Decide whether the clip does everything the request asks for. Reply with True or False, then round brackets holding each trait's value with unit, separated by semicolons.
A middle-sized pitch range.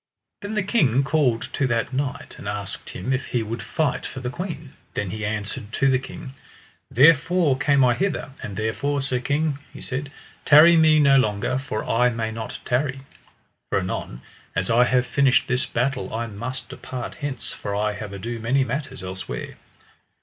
True (4.2 semitones)